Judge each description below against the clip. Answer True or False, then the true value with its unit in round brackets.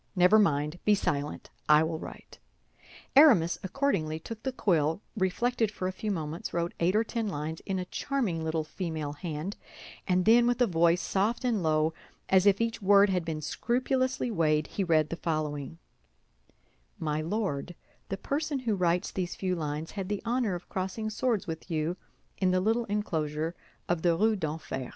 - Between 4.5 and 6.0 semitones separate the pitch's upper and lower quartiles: True (5.2 semitones)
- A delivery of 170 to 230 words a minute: True (175 wpm)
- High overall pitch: False (180 Hz)